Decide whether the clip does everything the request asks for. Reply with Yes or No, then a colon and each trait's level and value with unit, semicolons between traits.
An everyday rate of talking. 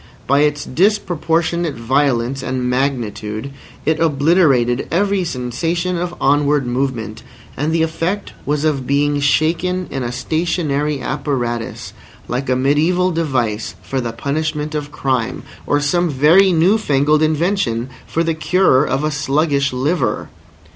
No: slow, 130 wpm